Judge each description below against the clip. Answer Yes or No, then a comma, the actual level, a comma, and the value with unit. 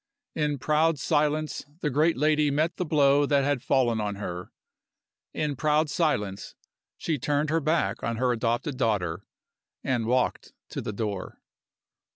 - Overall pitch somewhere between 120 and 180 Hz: Yes, medium, 140 Hz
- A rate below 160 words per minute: Yes, average, 150 wpm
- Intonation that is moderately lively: Yes, average, 4.7 semitones